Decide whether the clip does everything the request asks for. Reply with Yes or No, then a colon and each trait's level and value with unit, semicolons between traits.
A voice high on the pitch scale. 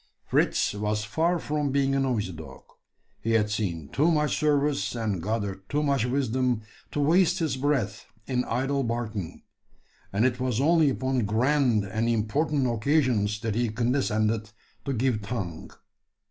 No: low, 120 Hz